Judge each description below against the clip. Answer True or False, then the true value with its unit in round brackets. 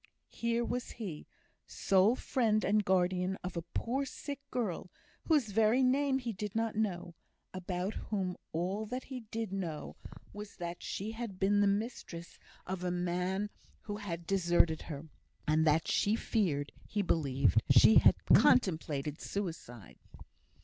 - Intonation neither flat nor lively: True (4.3 semitones)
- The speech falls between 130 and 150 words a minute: True (145 wpm)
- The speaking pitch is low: False (195 Hz)